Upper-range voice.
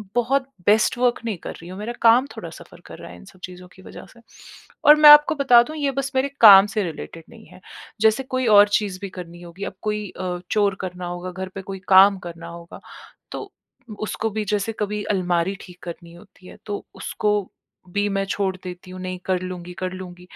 Yes: high, 195 Hz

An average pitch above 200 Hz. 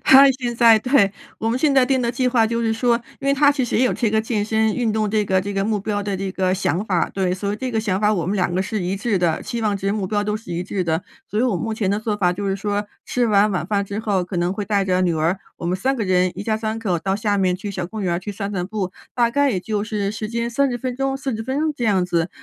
Yes: high, 210 Hz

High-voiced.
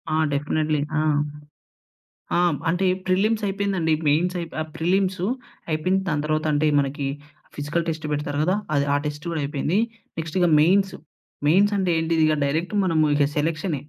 No: medium, 160 Hz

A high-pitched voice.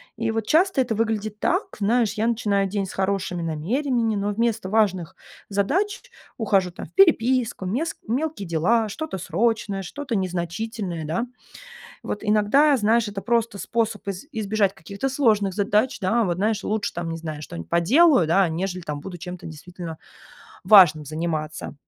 Yes: high, 205 Hz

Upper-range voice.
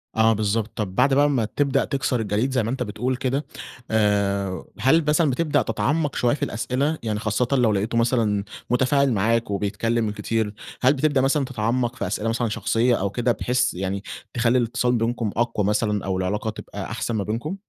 No: low, 115 Hz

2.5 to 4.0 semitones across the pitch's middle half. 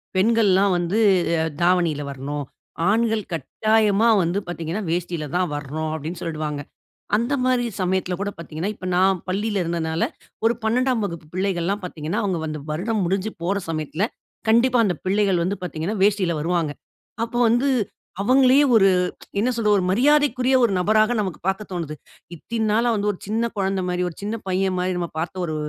No: average, 4.4 semitones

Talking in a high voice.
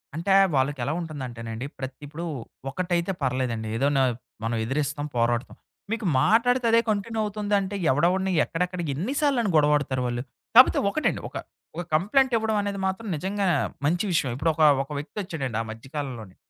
No: medium, 165 Hz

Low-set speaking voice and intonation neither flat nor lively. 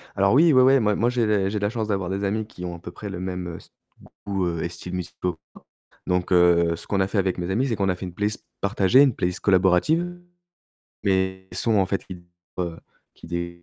Yes: very low, 95 Hz; average, 3.0 semitones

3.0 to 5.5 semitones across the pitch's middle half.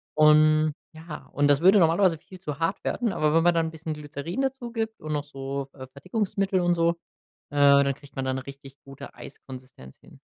Yes: average, 4.0 semitones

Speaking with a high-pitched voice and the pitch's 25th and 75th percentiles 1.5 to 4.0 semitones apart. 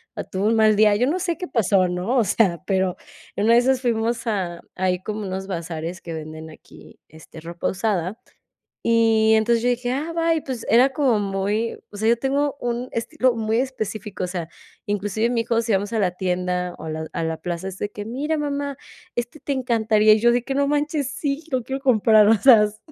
No: high, 220 Hz; average, 4.8 semitones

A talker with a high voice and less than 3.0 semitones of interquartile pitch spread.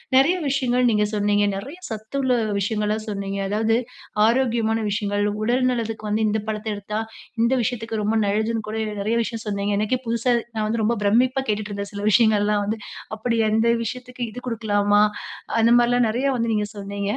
Yes: high, 220 Hz; narrow, 2.4 semitones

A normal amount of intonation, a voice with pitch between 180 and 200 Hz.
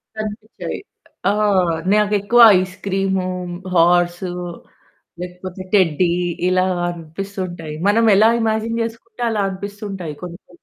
Yes: average, 3.1 semitones; high, 195 Hz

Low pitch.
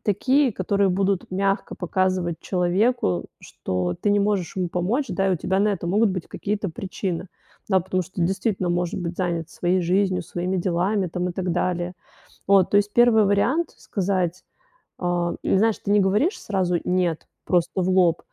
No: medium, 185 Hz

